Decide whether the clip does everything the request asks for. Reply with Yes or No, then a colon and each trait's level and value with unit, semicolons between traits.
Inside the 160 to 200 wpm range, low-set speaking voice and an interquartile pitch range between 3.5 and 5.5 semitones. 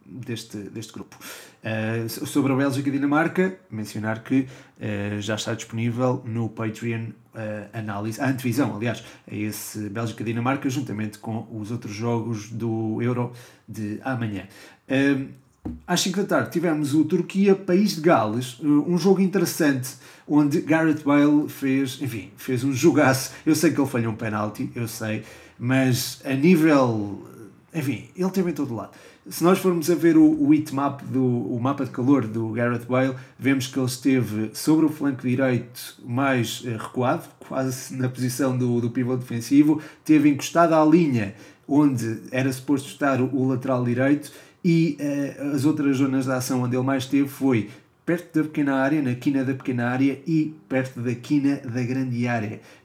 Yes: average, 170 wpm; low, 130 Hz; average, 4.0 semitones